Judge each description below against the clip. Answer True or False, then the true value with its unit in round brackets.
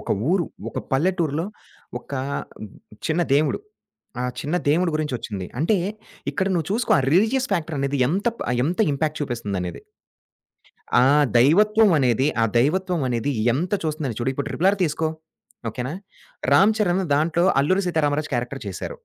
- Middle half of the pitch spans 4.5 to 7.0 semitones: True (5.1 semitones)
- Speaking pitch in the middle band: True (155 Hz)